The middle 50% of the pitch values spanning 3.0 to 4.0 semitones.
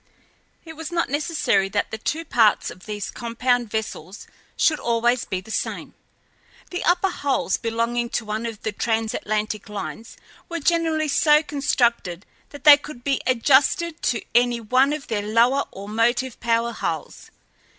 No: average, 4.7 semitones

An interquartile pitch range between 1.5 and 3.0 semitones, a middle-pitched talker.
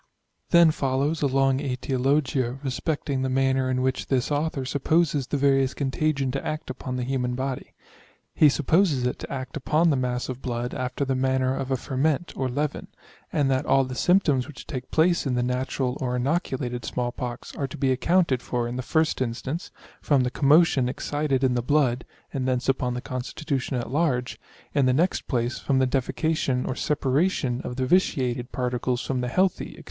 No: narrow, 2.4 semitones; low, 130 Hz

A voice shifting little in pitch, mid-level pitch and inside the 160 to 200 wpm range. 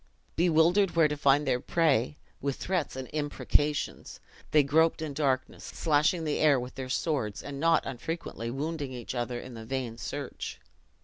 No: average, 3.6 semitones; medium, 145 Hz; average, 165 wpm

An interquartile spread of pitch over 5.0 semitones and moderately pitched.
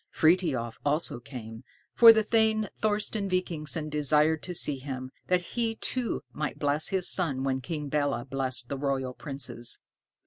Yes: wide, 5.6 semitones; medium, 150 Hz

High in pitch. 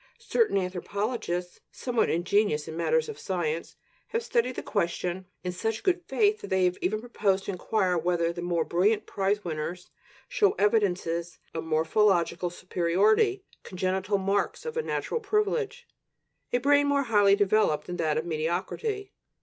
Yes: high, 195 Hz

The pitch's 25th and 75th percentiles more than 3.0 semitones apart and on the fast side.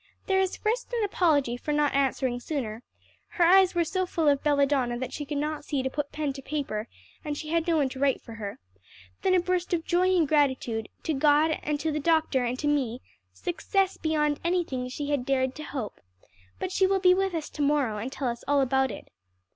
Yes: average, 4.2 semitones; fast, 220 wpm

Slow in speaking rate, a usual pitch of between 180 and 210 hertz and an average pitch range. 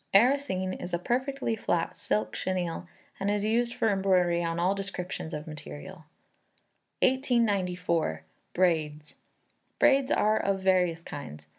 Yes: slow, 125 wpm; medium, 185 Hz; average, 4.1 semitones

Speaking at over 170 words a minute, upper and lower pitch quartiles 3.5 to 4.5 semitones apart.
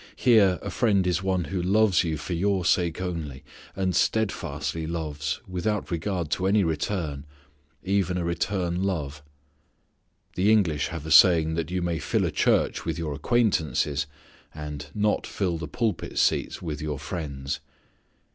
No: average, 155 wpm; average, 3.9 semitones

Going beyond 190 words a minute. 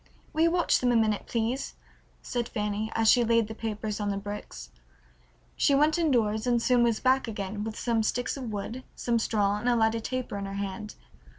Yes: fast, 205 wpm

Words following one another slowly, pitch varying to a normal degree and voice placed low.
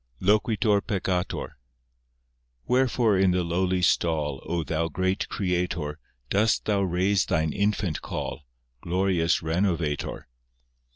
Yes: slow, 110 wpm; average, 3.3 semitones; very low, 90 Hz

